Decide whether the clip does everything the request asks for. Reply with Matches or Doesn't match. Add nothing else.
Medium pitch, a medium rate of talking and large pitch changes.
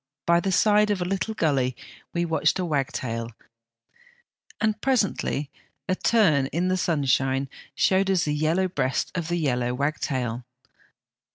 Matches